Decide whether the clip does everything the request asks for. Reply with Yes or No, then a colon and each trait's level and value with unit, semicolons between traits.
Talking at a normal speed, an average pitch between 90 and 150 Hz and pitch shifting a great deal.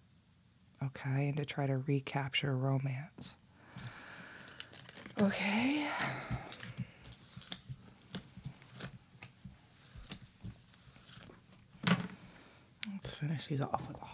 No: slow, 60 wpm; medium, 140 Hz; wide, 5.9 semitones